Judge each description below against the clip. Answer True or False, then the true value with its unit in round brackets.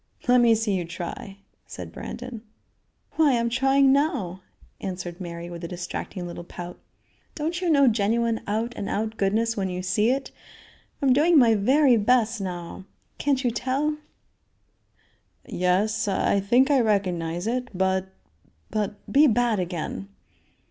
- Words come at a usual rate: True (145 wpm)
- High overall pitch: True (220 Hz)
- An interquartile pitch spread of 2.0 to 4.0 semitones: False (5.2 semitones)